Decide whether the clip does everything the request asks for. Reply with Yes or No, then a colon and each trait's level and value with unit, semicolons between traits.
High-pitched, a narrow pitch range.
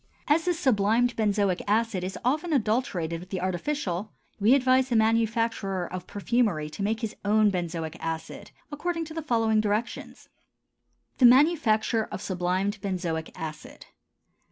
No: high, 215 Hz; average, 4.9 semitones